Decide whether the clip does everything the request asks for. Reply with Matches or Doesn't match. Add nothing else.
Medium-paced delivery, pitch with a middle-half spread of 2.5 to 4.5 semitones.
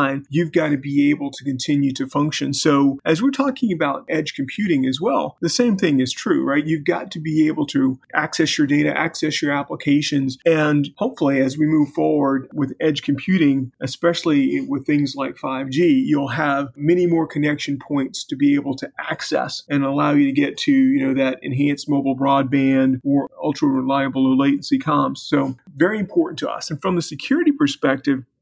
Matches